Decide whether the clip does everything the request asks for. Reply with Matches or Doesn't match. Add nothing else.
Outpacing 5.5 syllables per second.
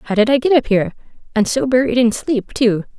Matches